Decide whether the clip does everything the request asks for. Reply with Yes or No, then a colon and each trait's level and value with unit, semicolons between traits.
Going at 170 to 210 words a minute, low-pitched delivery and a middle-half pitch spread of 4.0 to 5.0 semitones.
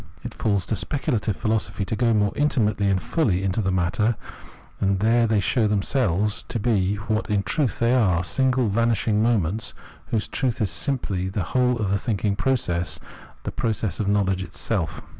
No: average, 180 wpm; low, 105 Hz; average, 3.3 semitones